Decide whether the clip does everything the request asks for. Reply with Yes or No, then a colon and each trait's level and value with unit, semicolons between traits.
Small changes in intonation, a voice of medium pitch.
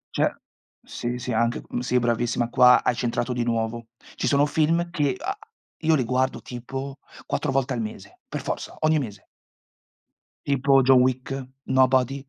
No: narrow, 2.3 semitones; low, 130 Hz